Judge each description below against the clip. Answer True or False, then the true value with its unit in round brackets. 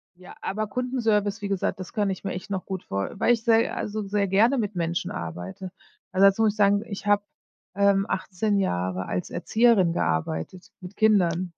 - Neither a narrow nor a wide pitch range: True (3.0 semitones)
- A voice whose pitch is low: False (195 Hz)